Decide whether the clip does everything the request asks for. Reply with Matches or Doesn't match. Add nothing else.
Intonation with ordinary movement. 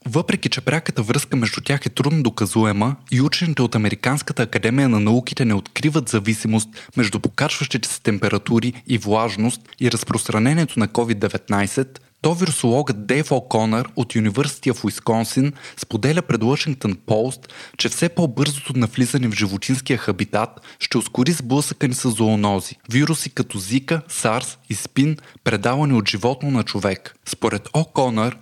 Matches